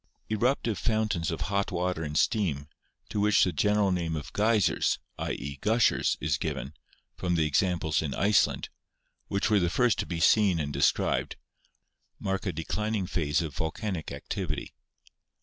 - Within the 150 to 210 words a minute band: Yes, average, 160 wpm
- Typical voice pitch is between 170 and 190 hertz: No, very low, 90 Hz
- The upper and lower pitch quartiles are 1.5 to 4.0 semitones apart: No, average, 4.7 semitones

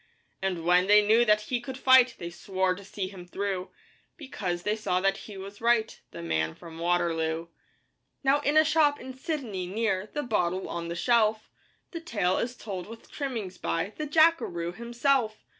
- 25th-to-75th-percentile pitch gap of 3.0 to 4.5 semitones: No, wide, 5.5 semitones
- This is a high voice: Yes, high, 210 Hz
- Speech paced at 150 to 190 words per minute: Yes, average, 180 wpm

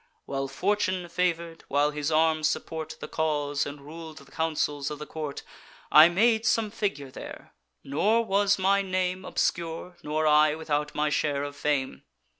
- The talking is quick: No, average, 160 wpm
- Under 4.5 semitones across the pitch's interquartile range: Yes, average, 3.6 semitones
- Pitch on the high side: No, medium, 160 Hz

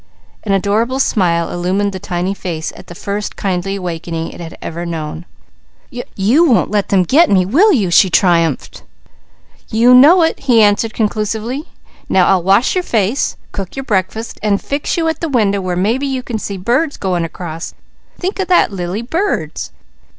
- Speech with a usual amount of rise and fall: No, wide, 5.8 semitones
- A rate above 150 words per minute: Yes, average, 175 wpm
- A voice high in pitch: Yes, high, 200 Hz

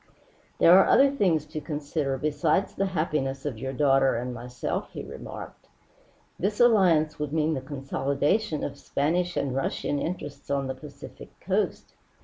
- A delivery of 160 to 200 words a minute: No, average, 150 wpm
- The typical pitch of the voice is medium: Yes, medium, 150 Hz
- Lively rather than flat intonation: No, average, 3.6 semitones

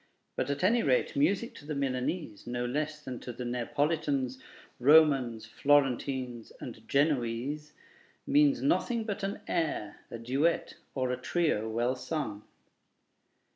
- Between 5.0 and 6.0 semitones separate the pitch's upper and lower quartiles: No, average, 4.2 semitones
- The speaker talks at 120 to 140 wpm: Yes, slow, 135 wpm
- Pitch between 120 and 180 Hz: Yes, medium, 140 Hz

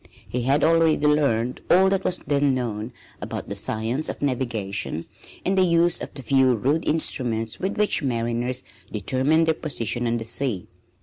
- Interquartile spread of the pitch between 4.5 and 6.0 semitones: Yes, average, 5.1 semitones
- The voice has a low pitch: Yes, low, 130 Hz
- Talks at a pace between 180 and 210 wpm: No, average, 170 wpm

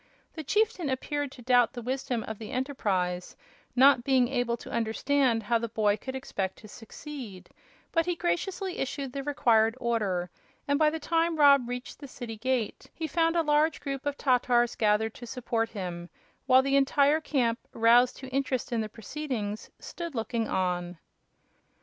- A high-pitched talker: Yes, very high, 250 Hz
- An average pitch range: Yes, average, 4.2 semitones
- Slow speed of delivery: No, average, 170 wpm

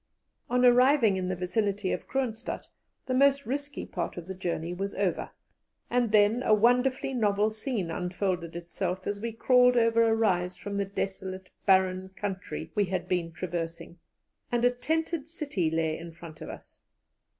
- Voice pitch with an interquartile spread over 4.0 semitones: Yes, average, 5.2 semitones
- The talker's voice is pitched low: No, high, 200 Hz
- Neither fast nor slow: Yes, average, 165 wpm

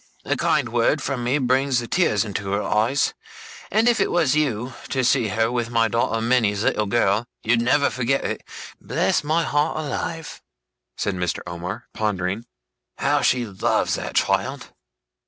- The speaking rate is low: No, average, 160 wpm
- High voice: No, low, 120 Hz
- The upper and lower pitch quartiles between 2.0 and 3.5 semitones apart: No, average, 4.6 semitones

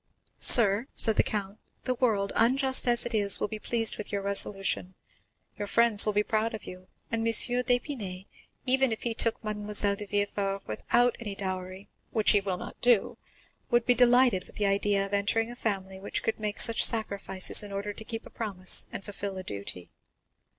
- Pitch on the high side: Yes, high, 210 Hz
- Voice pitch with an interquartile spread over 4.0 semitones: No, average, 2.8 semitones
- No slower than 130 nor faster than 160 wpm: No, average, 190 wpm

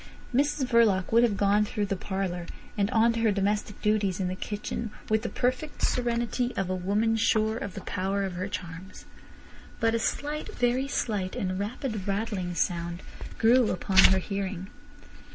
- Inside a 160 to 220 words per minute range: Yes, average, 170 wpm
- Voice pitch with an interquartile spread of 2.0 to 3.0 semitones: No, average, 3.4 semitones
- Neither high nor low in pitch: No, high, 205 Hz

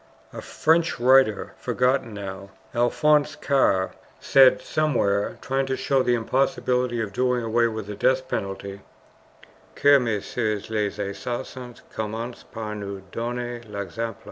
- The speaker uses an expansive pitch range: No, average, 3.7 semitones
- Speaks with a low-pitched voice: Yes, low, 120 Hz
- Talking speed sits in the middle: No, slow, 125 wpm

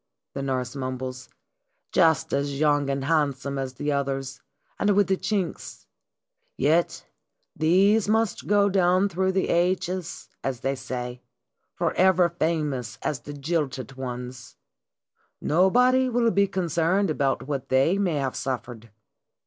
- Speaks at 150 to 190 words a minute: No, slow, 135 wpm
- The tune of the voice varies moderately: No, wide, 5.9 semitones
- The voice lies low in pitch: No, medium, 150 Hz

